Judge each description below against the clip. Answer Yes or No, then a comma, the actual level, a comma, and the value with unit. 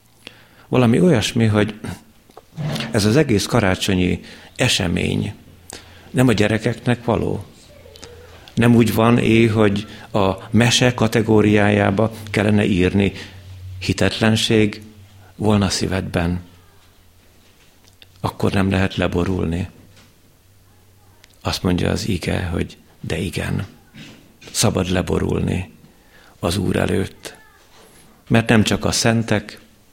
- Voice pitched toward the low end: Yes, low, 100 Hz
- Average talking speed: No, slow, 90 wpm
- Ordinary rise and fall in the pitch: Yes, average, 3.0 semitones